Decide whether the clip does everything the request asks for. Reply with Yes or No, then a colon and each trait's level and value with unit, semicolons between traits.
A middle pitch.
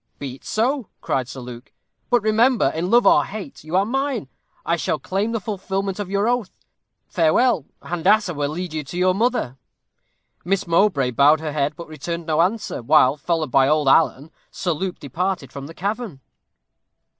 Yes: medium, 175 Hz